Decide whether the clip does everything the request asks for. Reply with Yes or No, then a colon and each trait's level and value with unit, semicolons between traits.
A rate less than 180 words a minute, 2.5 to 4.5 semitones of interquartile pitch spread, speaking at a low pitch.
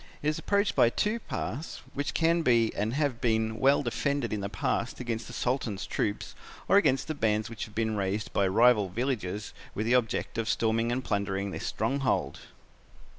No: average, 185 wpm; average, 3.9 semitones; low, 115 Hz